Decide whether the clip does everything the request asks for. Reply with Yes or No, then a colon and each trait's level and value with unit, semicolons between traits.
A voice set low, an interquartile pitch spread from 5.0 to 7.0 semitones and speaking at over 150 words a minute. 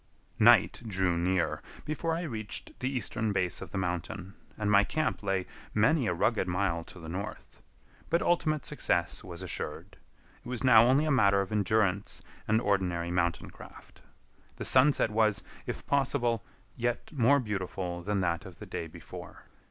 Yes: low, 100 Hz; average, 5.3 semitones; average, 165 wpm